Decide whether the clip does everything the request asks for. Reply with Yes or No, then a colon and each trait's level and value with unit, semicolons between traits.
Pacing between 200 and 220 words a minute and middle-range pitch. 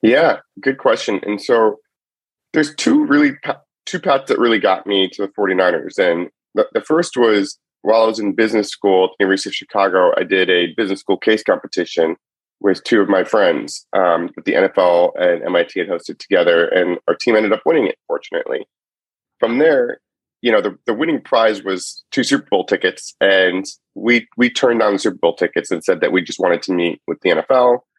Yes: fast, 205 wpm; medium, 155 Hz